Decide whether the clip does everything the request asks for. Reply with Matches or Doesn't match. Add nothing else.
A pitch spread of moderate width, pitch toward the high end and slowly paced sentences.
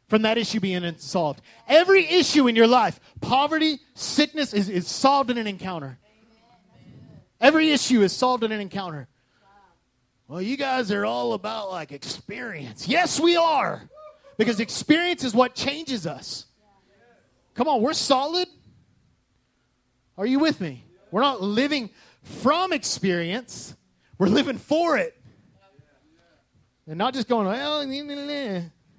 Doesn't match